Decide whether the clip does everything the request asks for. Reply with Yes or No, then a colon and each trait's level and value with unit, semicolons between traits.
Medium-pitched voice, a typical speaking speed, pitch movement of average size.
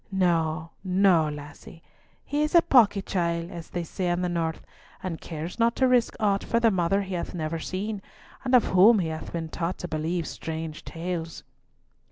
Yes: medium, 175 Hz; average, 190 wpm; average, 3.5 semitones